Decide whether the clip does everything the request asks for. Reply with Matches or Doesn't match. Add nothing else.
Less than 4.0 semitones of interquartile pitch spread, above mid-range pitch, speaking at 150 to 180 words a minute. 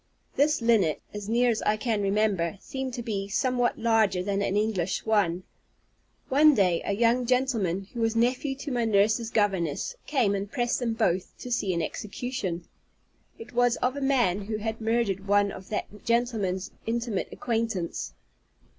Matches